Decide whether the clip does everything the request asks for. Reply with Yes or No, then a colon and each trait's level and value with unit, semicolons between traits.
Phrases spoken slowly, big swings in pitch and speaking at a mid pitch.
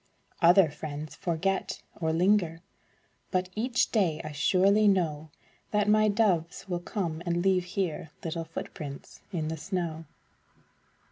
No: slow, 130 wpm; average, 3.5 semitones; medium, 175 Hz